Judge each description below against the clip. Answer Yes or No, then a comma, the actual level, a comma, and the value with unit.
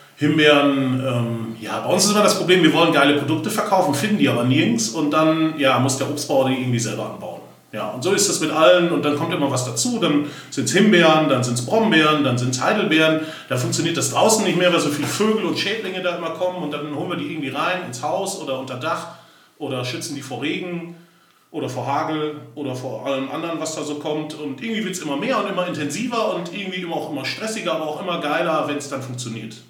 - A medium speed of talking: No, fast, 240 wpm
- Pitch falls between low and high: Yes, medium, 155 Hz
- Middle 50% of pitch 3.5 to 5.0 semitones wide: Yes, average, 3.8 semitones